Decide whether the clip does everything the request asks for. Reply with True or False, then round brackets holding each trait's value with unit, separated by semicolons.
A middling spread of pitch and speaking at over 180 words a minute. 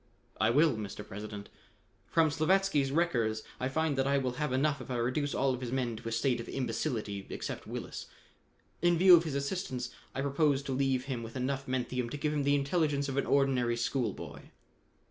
True (3.2 semitones; 200 wpm)